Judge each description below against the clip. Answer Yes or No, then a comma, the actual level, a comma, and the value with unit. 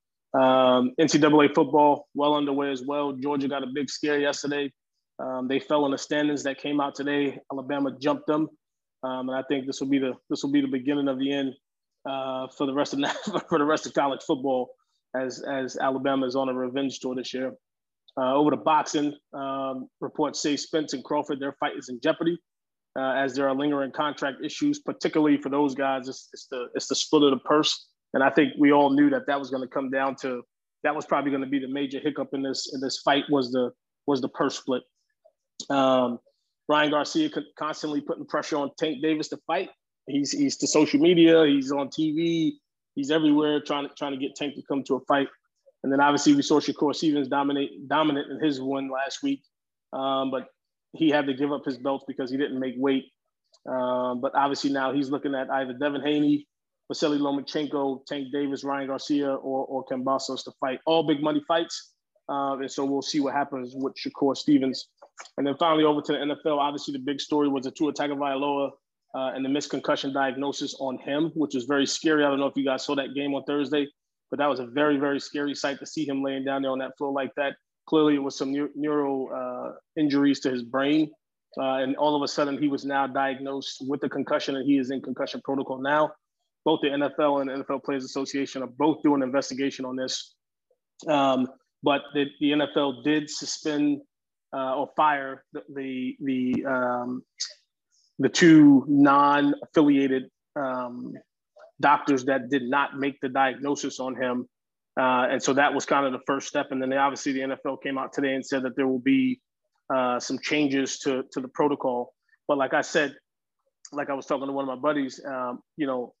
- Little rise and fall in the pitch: Yes, narrow, 1.7 semitones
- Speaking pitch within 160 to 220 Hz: No, medium, 140 Hz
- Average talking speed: No, fast, 210 wpm